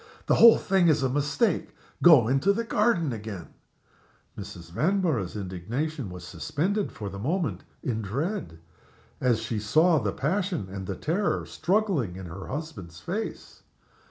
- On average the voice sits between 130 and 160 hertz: Yes, low, 135 Hz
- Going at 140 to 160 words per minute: Yes, average, 145 wpm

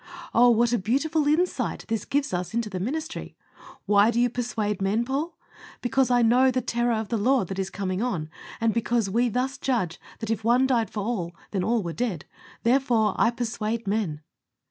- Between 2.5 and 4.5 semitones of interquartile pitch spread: Yes, average, 3.1 semitones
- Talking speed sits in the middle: Yes, average, 195 wpm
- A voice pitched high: Yes, high, 230 Hz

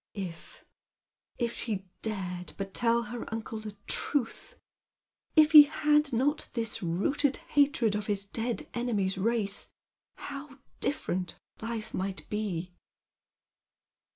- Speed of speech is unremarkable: No, slow, 120 wpm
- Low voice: No, high, 225 Hz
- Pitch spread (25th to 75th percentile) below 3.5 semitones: No, average, 5.1 semitones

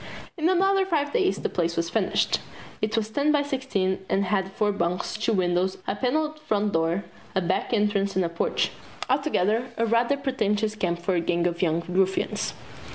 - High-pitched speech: Yes, high, 205 Hz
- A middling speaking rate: Yes, average, 185 wpm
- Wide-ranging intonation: Yes, wide, 6.1 semitones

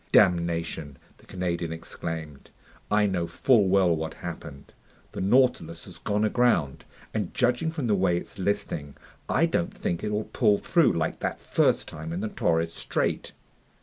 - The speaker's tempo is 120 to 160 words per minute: Yes, average, 155 wpm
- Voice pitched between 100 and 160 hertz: No, very low, 90 Hz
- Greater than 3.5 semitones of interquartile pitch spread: Yes, average, 4.6 semitones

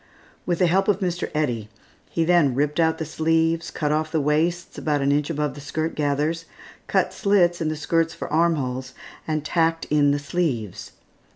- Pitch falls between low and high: Yes, medium, 155 Hz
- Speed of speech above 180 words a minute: Yes, average, 190 wpm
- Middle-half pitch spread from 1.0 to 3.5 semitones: Yes, narrow, 2.4 semitones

